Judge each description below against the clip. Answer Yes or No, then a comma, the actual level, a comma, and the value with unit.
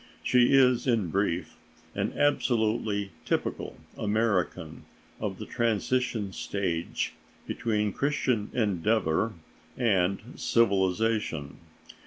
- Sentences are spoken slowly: Yes, slow, 85 wpm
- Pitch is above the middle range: No, low, 105 Hz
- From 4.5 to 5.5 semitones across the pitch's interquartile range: No, average, 3.6 semitones